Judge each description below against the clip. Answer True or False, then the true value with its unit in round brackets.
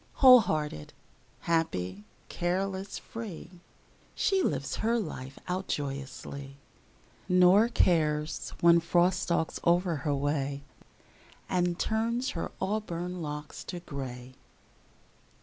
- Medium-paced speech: False (100 wpm)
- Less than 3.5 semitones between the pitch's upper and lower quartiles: False (4.6 semitones)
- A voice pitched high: False (170 Hz)